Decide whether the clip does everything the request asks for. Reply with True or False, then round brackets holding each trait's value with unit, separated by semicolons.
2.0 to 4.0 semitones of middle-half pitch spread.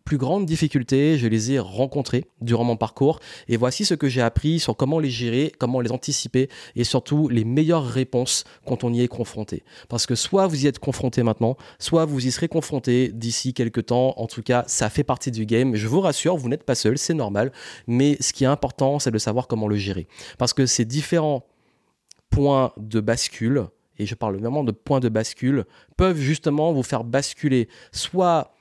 True (3.6 semitones)